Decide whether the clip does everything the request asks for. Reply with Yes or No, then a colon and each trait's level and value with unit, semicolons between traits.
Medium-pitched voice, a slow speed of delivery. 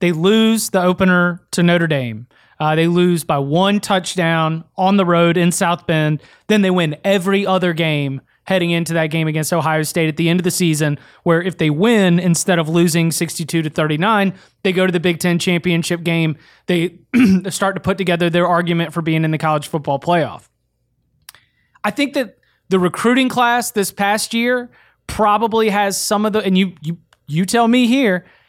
No: medium, 175 Hz; average, 190 wpm